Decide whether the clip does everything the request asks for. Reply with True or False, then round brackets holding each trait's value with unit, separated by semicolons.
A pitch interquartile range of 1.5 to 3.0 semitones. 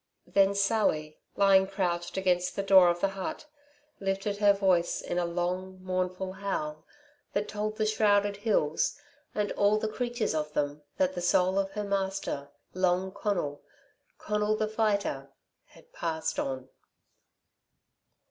True (2.7 semitones)